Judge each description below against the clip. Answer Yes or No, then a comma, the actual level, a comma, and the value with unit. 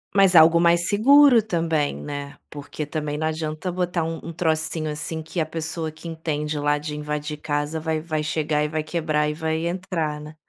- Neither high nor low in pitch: Yes, medium, 155 Hz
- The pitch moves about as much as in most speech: No, narrow, 1.9 semitones